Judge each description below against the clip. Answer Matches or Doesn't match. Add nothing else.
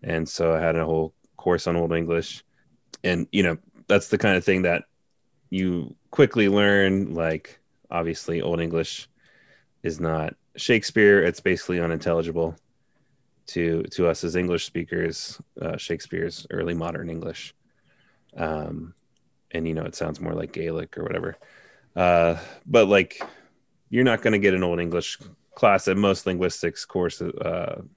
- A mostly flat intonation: Matches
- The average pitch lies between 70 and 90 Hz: Matches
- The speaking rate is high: Doesn't match